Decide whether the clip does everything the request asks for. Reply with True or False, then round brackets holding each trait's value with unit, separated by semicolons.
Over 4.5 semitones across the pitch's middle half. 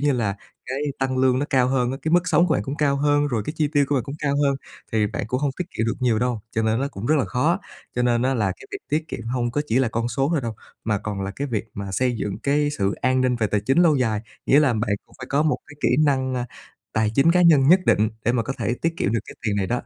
False (4.2 semitones)